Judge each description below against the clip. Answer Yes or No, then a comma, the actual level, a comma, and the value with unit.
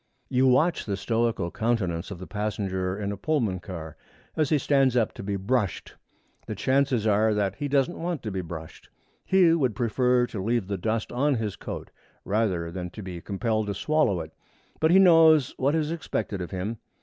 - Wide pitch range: Yes, wide, 5.8 semitones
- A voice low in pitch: Yes, low, 110 Hz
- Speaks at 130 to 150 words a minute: No, average, 195 wpm